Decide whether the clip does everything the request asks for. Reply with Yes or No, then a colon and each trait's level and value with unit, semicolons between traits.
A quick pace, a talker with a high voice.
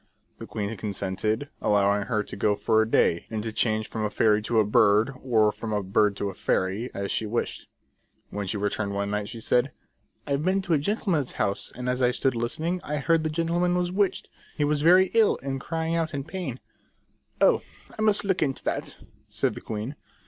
No: fast, 215 wpm; low, 120 Hz